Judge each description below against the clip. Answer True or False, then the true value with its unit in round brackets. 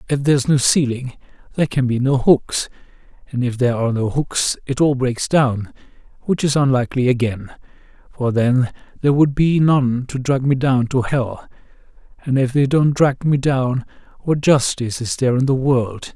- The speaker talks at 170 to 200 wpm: True (180 wpm)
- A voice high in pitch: False (130 Hz)